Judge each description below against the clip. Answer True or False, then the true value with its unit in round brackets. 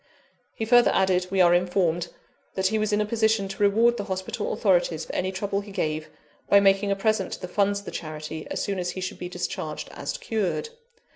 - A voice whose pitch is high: True (195 Hz)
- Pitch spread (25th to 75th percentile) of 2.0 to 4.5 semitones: True (2.9 semitones)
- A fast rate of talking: True (220 wpm)